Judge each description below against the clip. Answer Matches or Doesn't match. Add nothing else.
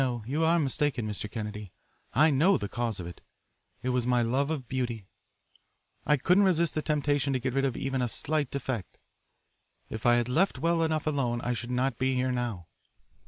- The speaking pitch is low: Matches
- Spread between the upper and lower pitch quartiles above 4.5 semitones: Doesn't match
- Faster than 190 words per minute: Matches